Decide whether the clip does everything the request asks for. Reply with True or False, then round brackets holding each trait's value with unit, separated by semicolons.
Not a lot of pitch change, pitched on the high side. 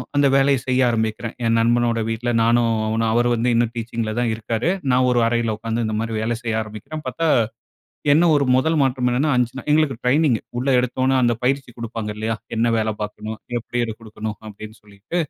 False (2.3 semitones; 115 Hz)